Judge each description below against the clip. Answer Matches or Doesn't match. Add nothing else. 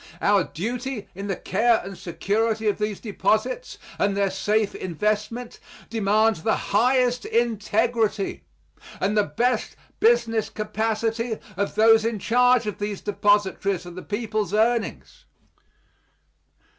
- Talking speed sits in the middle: Doesn't match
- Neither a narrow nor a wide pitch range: Doesn't match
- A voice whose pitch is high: Matches